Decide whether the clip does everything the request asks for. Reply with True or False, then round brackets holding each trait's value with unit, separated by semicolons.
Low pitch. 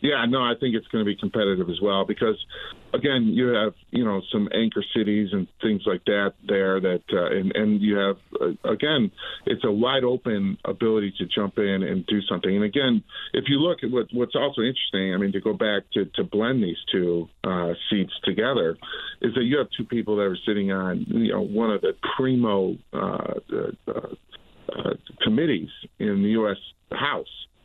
True (105 Hz)